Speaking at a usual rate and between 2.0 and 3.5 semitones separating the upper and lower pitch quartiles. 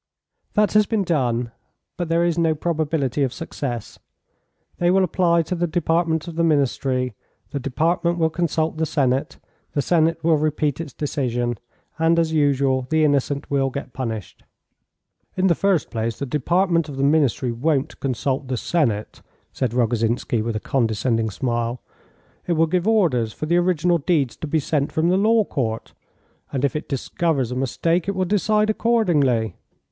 No: average, 170 wpm; average, 4.9 semitones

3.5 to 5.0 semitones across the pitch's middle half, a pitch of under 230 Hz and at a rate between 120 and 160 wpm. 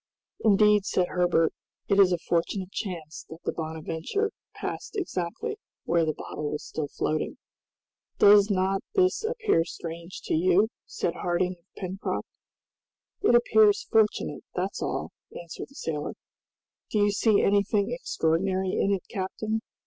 Yes: average, 3.8 semitones; high, 190 Hz; average, 140 wpm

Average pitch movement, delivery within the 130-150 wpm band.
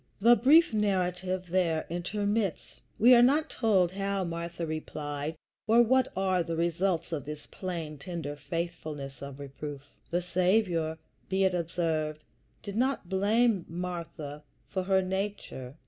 Yes: average, 3.8 semitones; slow, 135 wpm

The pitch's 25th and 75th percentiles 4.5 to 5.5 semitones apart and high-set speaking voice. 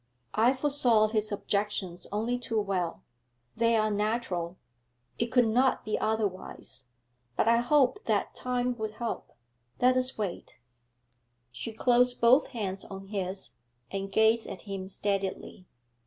No: average, 3.6 semitones; high, 220 Hz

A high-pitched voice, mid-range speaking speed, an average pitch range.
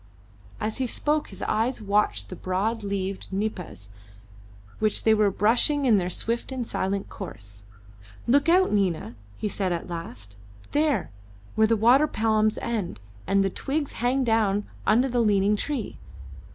Yes: high, 215 Hz; average, 150 wpm; average, 3.9 semitones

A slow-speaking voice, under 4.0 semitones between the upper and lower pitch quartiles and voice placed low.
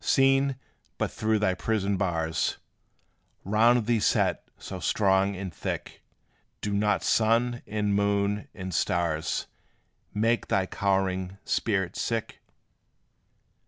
Yes: slow, 110 wpm; average, 2.7 semitones; low, 100 Hz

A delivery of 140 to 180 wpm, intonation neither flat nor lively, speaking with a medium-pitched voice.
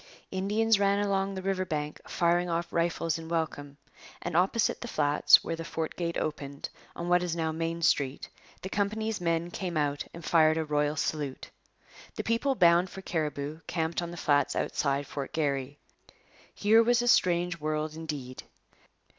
Yes: average, 170 wpm; average, 3.6 semitones; medium, 165 Hz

